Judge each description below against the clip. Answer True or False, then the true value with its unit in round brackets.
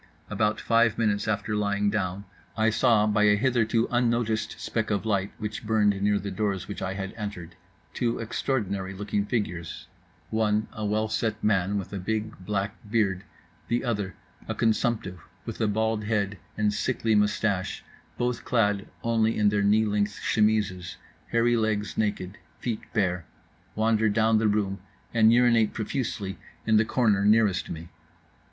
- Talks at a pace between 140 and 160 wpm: True (150 wpm)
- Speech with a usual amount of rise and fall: False (1.8 semitones)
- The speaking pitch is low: True (105 Hz)